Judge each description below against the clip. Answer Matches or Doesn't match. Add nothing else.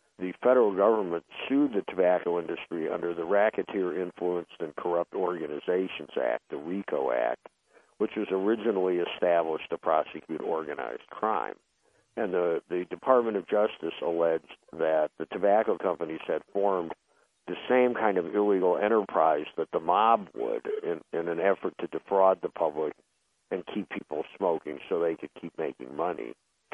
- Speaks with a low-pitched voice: Matches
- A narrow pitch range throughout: Doesn't match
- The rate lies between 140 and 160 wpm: Matches